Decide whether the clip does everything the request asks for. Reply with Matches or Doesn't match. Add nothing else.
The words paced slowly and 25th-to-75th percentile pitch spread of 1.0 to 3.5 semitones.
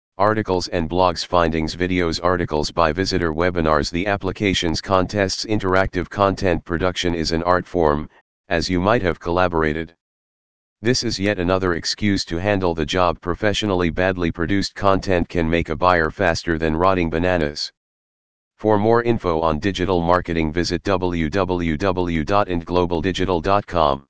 Matches